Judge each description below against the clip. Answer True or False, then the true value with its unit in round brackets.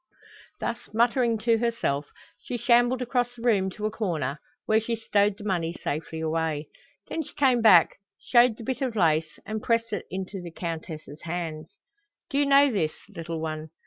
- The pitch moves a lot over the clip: True (6.6 semitones)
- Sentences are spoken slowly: False (175 wpm)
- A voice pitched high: True (210 Hz)